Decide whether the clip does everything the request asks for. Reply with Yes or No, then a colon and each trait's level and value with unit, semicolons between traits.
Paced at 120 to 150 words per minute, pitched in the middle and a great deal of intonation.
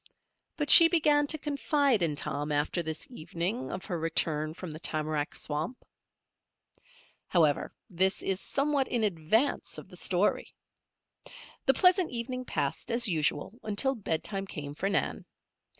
No: average, 140 wpm; high, 195 Hz; wide, 8.9 semitones